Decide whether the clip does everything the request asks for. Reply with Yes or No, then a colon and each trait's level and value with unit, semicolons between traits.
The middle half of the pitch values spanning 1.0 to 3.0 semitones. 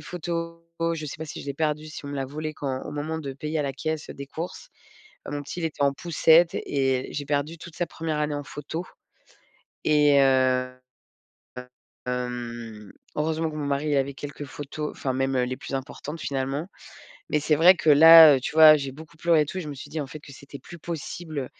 Yes: narrow, 2.6 semitones